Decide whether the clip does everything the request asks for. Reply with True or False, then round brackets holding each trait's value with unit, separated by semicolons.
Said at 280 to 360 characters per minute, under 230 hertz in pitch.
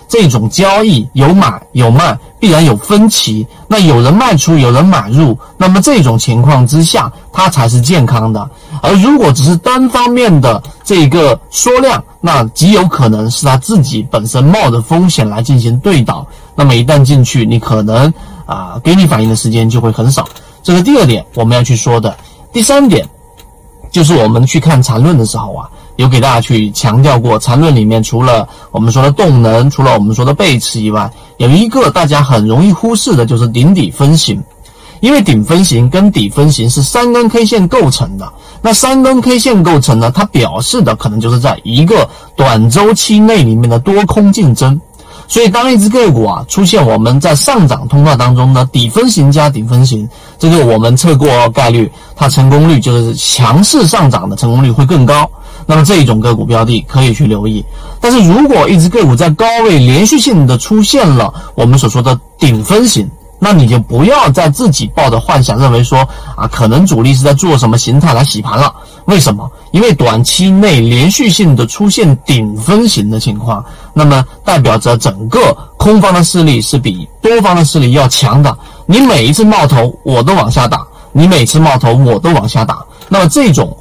True (285 characters per minute; 140 Hz)